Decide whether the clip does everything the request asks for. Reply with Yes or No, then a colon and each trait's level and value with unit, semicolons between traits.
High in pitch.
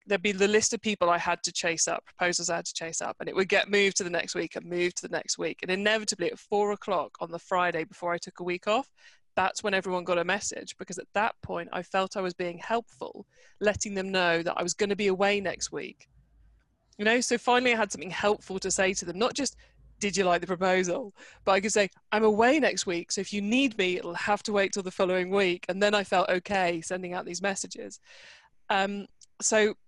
Yes: high, 195 Hz